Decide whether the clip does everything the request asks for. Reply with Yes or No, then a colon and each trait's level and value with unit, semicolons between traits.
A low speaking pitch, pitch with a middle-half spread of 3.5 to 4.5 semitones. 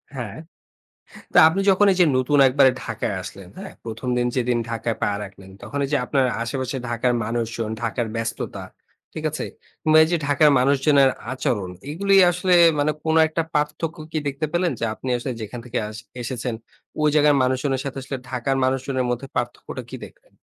Yes: low, 130 Hz; average, 4.0 semitones